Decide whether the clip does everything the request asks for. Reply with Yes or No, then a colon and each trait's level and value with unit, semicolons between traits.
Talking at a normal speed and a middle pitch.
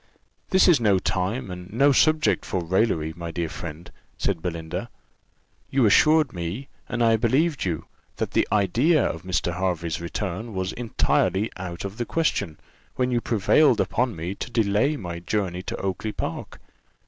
No: average, 160 wpm; low, 100 Hz